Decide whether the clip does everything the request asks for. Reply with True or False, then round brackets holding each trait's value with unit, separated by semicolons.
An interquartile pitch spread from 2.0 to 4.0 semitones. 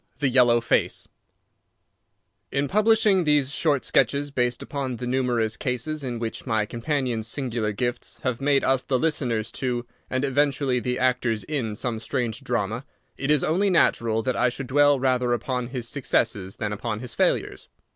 True (3.1 semitones)